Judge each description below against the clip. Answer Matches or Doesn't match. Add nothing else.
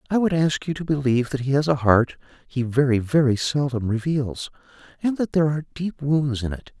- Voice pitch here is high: Doesn't match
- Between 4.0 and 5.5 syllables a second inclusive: Doesn't match